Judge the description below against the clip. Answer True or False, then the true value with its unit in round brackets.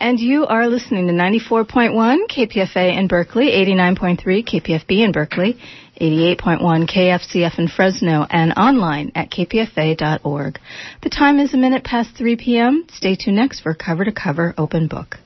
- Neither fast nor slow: True (150 wpm)